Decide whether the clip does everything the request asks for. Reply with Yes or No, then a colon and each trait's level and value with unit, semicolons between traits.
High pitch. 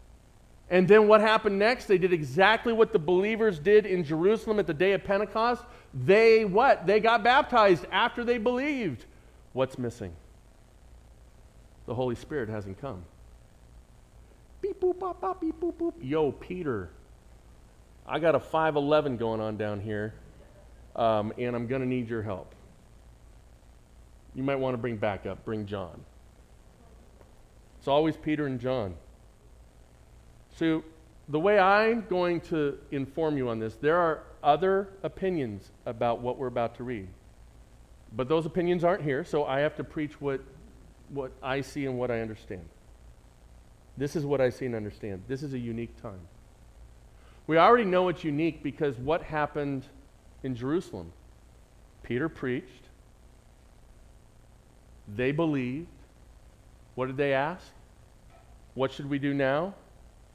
No: low, 135 Hz